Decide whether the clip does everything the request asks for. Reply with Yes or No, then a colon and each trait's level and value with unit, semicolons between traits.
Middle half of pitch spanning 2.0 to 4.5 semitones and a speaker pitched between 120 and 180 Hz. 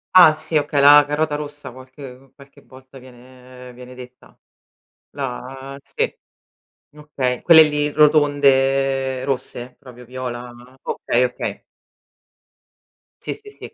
Yes: narrow, 2.5 semitones; low, 135 Hz